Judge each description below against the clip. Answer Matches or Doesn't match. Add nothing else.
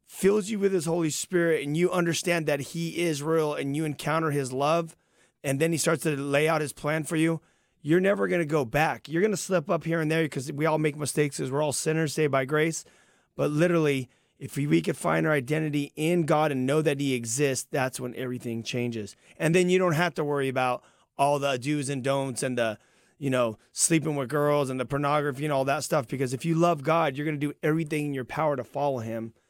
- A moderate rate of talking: Doesn't match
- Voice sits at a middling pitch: Matches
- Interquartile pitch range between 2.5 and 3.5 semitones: Matches